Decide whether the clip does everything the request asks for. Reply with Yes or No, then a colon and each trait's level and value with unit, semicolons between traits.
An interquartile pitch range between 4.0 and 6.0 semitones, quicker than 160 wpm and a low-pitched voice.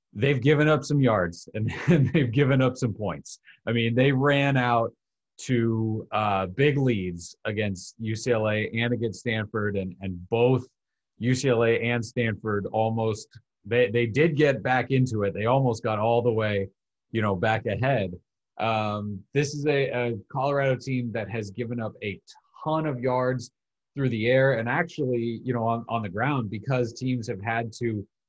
No: average, 3.0 semitones; average, 170 wpm; low, 120 Hz